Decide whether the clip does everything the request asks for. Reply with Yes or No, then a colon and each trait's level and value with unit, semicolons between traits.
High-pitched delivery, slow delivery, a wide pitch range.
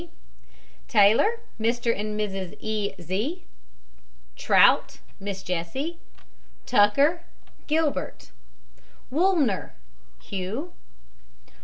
Yes: high, 220 Hz; slow, 70 wpm; wide, 7.5 semitones